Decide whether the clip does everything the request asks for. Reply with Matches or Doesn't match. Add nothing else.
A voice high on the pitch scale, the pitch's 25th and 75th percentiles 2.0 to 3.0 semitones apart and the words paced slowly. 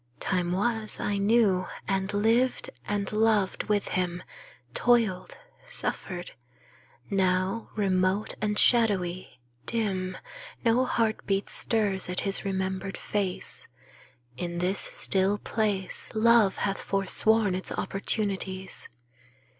Matches